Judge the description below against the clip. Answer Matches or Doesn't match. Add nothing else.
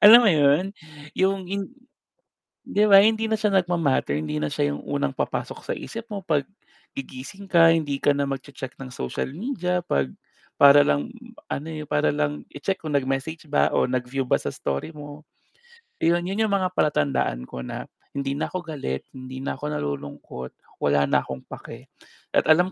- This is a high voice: Doesn't match